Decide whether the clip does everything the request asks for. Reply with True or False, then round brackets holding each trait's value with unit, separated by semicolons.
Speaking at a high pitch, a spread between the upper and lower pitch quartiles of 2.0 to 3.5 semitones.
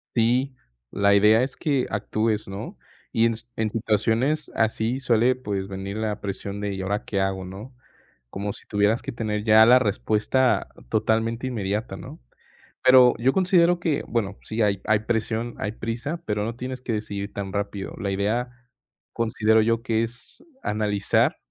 False (110 Hz; 2.8 semitones)